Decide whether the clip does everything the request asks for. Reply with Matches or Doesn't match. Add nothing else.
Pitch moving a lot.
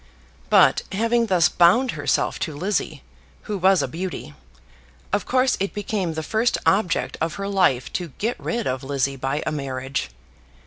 Matches